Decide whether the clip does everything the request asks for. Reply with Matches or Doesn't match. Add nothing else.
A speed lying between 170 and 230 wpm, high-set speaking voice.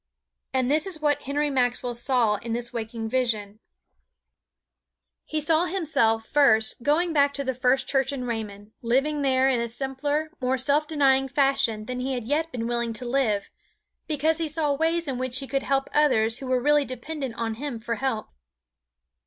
Matches